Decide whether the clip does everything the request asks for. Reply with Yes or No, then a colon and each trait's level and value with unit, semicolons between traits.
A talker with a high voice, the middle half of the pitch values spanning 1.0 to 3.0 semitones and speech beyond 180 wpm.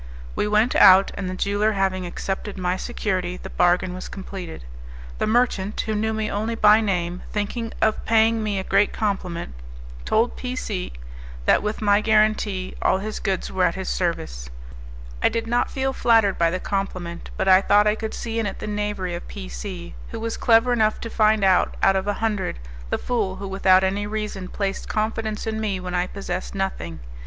Yes: high, 205 Hz; average, 2.7 semitones; average, 195 wpm